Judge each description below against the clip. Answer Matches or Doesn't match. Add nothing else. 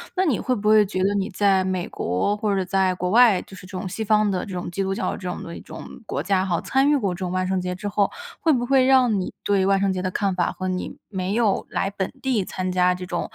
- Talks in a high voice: Matches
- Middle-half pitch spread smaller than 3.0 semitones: Matches